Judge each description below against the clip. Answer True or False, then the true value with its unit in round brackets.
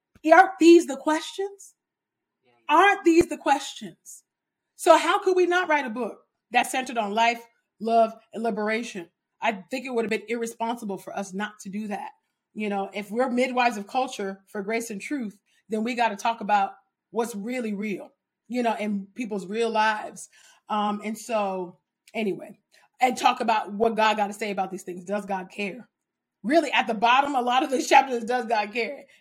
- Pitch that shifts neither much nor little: True (3.8 semitones)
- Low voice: False (225 Hz)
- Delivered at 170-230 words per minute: True (190 wpm)